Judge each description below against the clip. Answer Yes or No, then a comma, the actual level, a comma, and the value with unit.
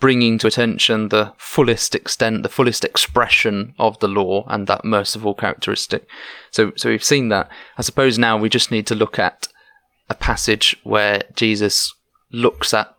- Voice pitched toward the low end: Yes, low, 110 Hz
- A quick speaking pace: No, average, 165 wpm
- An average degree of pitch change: No, narrow, 2.3 semitones